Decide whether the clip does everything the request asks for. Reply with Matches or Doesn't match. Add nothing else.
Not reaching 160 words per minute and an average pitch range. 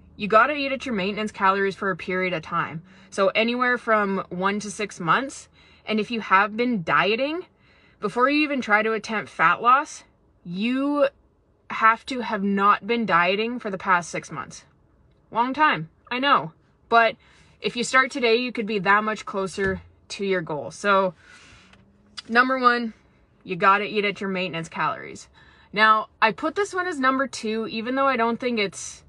Doesn't match